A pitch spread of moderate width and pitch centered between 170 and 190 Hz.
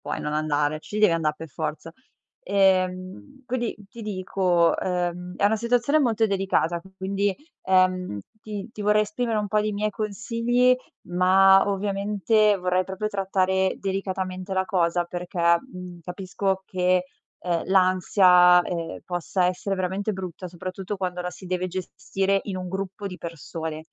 No: narrow, 2.2 semitones; medium, 185 Hz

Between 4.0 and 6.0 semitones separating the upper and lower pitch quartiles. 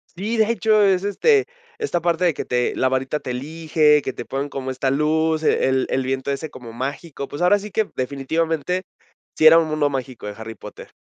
Yes: average, 4.7 semitones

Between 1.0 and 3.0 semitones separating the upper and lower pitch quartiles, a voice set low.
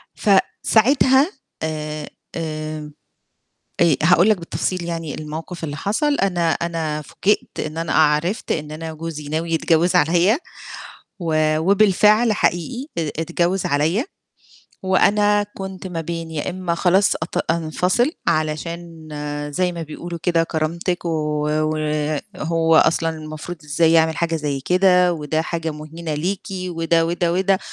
No: average, 2.7 semitones; medium, 165 Hz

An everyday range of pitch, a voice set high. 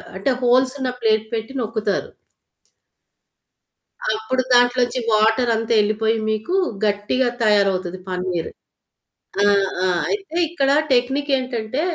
Yes: average, 3.2 semitones; high, 225 Hz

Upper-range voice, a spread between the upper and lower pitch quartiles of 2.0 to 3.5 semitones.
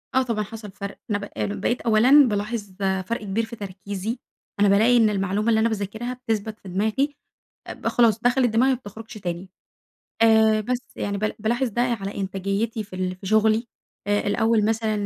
Yes: high, 215 Hz; narrow, 2.6 semitones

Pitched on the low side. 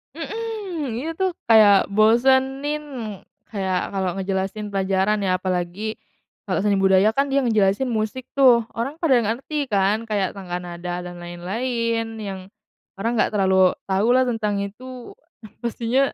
No: high, 215 Hz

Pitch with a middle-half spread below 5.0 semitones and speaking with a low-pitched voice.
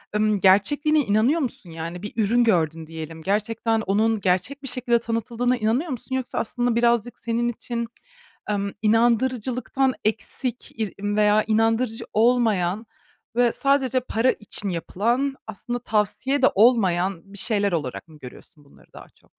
No: average, 3.4 semitones; high, 225 Hz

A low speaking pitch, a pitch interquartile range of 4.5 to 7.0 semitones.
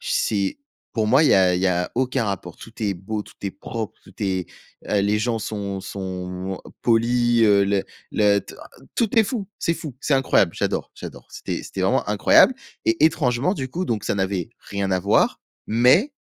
Yes: low, 105 Hz; average, 4.8 semitones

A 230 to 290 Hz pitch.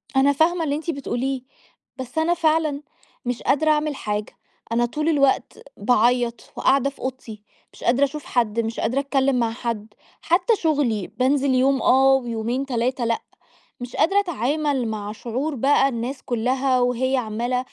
Yes: very high, 260 Hz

